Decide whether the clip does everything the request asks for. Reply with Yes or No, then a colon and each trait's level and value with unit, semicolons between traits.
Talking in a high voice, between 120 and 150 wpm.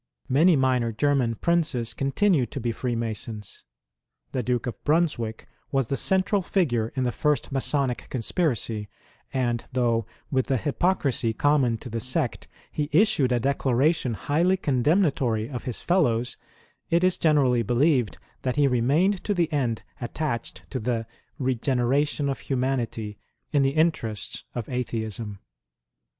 No: low, 130 Hz; average, 140 wpm